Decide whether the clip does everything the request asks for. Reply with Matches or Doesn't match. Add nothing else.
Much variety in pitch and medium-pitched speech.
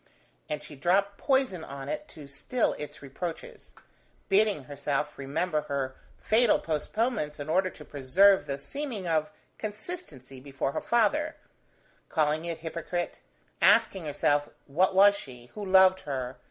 Matches